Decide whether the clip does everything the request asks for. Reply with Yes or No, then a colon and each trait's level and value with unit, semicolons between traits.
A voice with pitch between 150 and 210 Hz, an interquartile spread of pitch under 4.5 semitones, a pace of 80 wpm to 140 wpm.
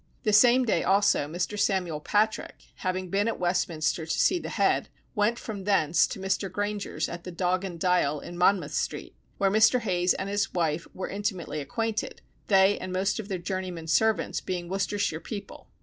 No: high, 190 Hz; average, 2.8 semitones; average, 180 wpm